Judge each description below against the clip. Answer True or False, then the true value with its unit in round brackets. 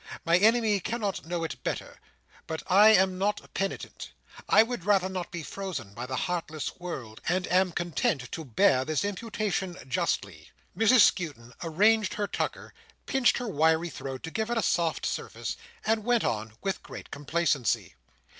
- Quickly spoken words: False (165 wpm)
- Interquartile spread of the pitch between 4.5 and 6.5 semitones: True (4.9 semitones)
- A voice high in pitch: False (180 Hz)